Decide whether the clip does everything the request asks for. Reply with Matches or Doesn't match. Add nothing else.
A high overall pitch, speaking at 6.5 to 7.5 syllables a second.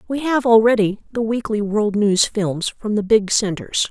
Doesn't match